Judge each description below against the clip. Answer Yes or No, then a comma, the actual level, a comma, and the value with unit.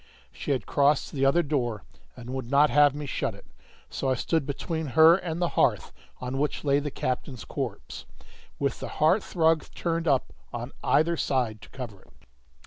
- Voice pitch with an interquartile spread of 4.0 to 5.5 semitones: No, average, 3.6 semitones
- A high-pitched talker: No, medium, 140 Hz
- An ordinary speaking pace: Yes, average, 185 wpm